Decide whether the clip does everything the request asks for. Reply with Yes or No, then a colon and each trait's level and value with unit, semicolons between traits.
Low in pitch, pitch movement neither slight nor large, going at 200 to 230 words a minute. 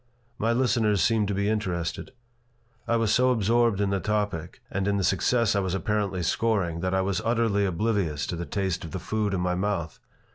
Yes: low, 100 Hz; average, 3.0 semitones; fast, 205 wpm